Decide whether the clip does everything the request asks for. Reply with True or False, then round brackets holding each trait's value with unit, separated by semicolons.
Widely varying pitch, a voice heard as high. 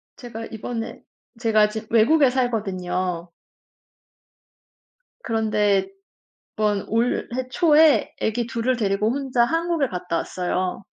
False (3.8 semitones; 225 Hz)